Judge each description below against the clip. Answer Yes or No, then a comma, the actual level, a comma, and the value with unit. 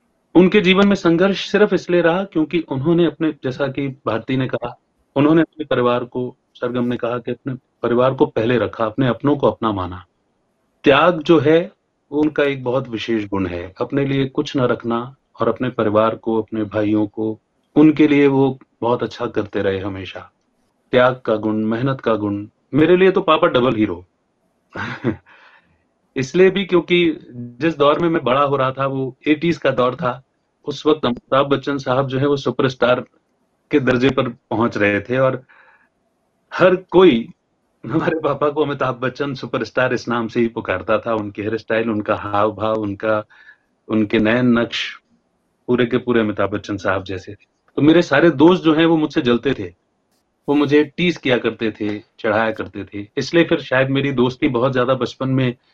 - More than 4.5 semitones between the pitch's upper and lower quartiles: Yes, average, 5.1 semitones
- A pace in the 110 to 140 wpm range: No, average, 180 wpm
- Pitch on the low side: Yes, low, 130 Hz